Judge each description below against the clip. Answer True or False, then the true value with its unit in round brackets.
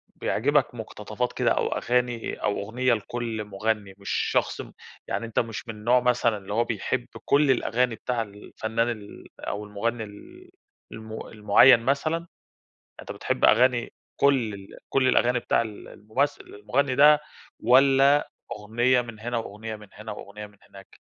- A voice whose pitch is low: True (115 Hz)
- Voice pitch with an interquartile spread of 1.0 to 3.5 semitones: True (3.1 semitones)